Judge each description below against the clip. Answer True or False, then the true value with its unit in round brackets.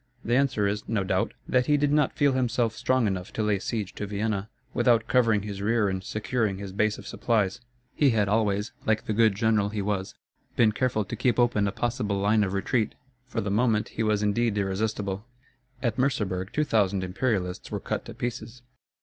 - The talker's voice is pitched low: True (110 Hz)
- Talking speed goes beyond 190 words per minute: True (200 wpm)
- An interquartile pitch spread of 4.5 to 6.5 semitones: False (3.0 semitones)